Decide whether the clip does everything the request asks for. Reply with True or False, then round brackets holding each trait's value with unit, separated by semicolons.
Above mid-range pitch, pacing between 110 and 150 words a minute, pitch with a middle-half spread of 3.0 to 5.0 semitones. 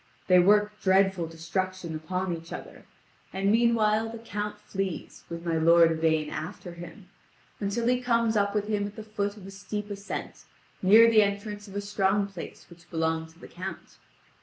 False (195 Hz; 180 wpm; 3.4 semitones)